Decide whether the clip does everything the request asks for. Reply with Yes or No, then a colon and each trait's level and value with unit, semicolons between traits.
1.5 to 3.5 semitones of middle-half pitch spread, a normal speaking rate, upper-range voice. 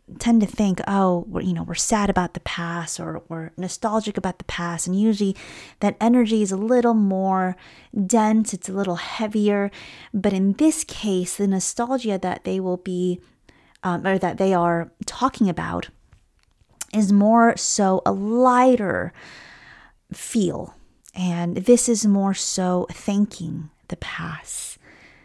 Yes: average, 3.2 semitones; average, 145 wpm; high, 195 Hz